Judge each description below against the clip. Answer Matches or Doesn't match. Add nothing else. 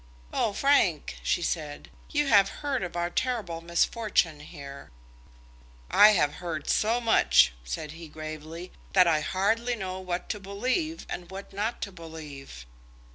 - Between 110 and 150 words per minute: Matches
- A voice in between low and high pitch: Matches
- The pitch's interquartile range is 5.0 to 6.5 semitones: Matches